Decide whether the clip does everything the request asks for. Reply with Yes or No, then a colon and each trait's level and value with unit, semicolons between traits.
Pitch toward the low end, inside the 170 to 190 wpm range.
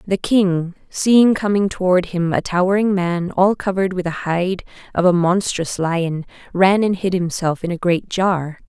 No: medium, 185 Hz; average, 180 wpm